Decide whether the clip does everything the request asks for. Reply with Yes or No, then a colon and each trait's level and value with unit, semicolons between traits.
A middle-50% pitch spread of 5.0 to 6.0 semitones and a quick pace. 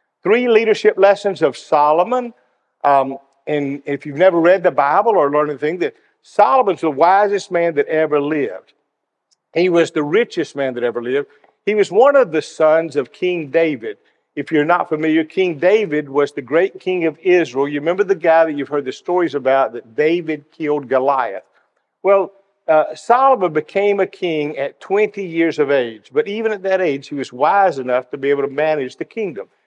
No: average, 5.3 semitones; average, 190 wpm